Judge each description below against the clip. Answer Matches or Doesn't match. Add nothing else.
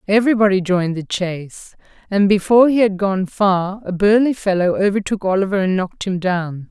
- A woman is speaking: Matches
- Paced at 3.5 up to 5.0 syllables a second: Doesn't match